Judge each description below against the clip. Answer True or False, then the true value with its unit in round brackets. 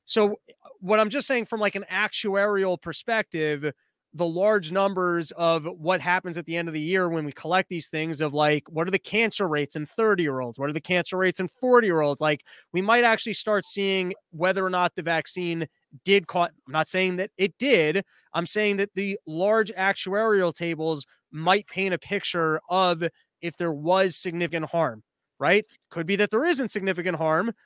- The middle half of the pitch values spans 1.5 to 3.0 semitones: False (3.5 semitones)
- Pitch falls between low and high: True (180 Hz)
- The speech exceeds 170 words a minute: True (195 wpm)